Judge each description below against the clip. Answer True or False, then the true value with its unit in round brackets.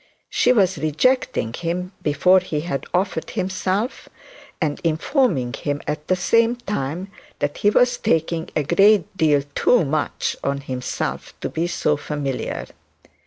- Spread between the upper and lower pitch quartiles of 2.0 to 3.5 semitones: False (5.0 semitones)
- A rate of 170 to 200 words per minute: False (140 wpm)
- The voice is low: False (165 Hz)